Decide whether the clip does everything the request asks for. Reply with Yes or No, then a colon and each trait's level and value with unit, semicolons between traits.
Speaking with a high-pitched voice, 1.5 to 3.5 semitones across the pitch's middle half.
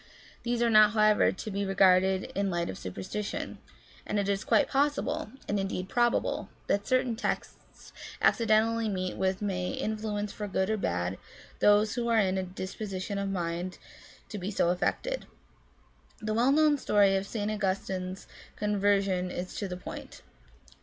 Yes: high, 200 Hz; narrow, 2.5 semitones